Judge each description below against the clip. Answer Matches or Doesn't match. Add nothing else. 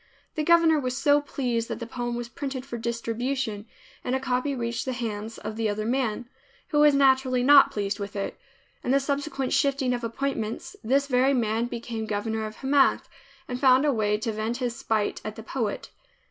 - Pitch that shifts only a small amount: Doesn't match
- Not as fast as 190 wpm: Doesn't match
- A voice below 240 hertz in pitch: Doesn't match